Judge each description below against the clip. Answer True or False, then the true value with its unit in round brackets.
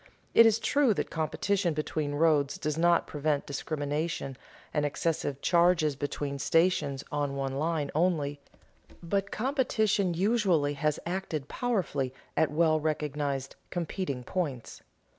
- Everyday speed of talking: False (125 wpm)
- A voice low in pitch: False (155 Hz)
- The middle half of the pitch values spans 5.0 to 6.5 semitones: False (3.9 semitones)